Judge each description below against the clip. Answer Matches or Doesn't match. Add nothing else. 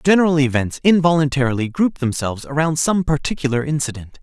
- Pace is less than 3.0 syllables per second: Doesn't match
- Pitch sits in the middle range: Matches